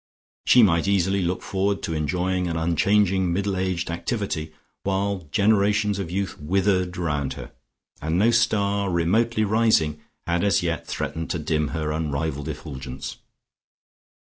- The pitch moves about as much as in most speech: Yes, average, 3.6 semitones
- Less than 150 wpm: Yes, average, 140 wpm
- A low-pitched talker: Yes, very low, 90 Hz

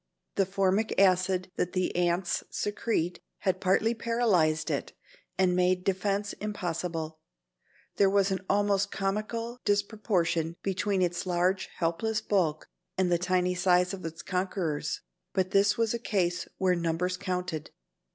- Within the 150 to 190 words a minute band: No, slow, 135 wpm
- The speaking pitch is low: No, medium, 185 Hz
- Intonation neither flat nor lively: No, narrow, 2.2 semitones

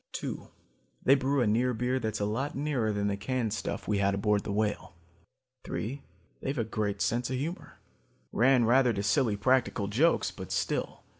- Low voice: Yes, low, 115 Hz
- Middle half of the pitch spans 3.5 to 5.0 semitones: Yes, average, 4.0 semitones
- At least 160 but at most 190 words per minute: Yes, average, 180 wpm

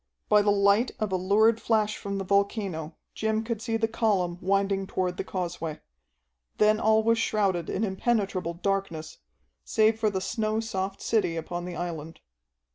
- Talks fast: No, average, 165 wpm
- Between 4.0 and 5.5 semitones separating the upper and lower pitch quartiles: No, average, 3.2 semitones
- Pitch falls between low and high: No, high, 200 Hz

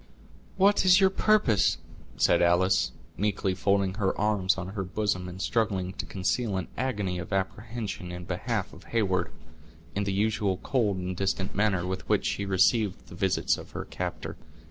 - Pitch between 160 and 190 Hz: No, low, 100 Hz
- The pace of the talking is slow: No, average, 165 wpm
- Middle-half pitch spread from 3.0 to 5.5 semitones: No, narrow, 2.6 semitones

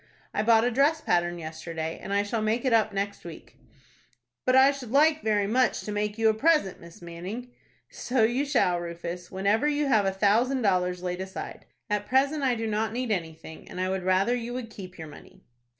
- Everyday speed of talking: No, fast, 210 wpm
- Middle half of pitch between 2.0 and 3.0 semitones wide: No, average, 5.3 semitones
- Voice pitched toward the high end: Yes, high, 210 Hz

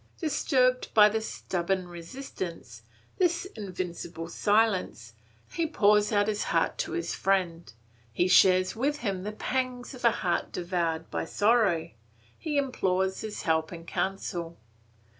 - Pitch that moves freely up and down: Yes, wide, 5.9 semitones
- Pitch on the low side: No, high, 195 Hz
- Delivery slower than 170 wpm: Yes, slow, 135 wpm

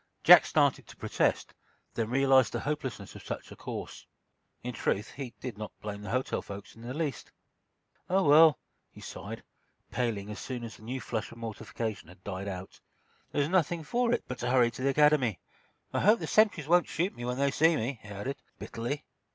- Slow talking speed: No, average, 195 wpm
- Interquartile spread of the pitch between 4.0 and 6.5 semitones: Yes, average, 5.2 semitones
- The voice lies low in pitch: Yes, low, 125 Hz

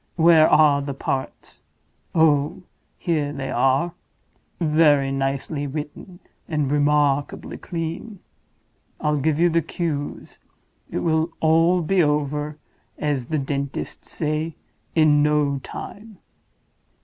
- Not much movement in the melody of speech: Yes, narrow, 2.3 semitones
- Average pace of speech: No, slow, 105 wpm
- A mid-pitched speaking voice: Yes, medium, 150 Hz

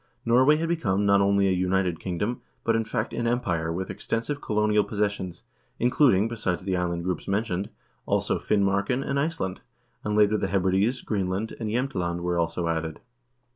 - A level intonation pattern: No, average, 3.9 semitones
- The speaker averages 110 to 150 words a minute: No, average, 170 wpm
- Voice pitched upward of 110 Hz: No, low, 100 Hz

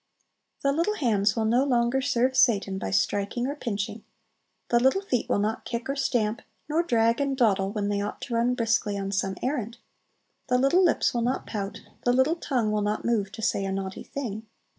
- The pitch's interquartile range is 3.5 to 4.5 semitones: Yes, average, 4.2 semitones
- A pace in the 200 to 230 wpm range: Yes, fast, 205 wpm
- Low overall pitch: No, high, 235 Hz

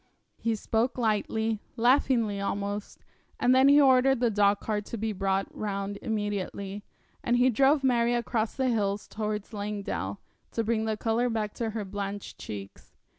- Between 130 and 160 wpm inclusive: Yes, average, 155 wpm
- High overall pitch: Yes, high, 220 Hz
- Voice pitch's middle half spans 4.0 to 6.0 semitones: No, average, 2.8 semitones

